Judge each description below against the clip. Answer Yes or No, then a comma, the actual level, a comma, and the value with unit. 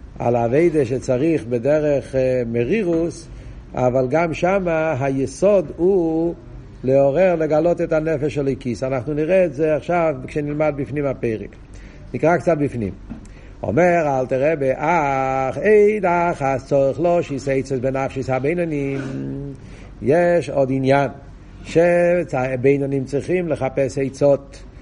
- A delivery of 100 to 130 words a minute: Yes, average, 120 wpm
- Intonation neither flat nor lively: Yes, average, 4.0 semitones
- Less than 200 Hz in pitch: Yes, medium, 140 Hz